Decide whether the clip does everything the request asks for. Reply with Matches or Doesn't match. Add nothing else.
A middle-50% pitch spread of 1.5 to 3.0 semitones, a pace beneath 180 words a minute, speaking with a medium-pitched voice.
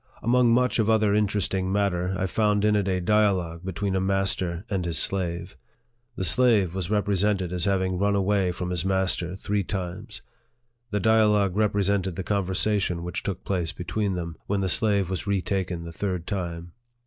Doesn't match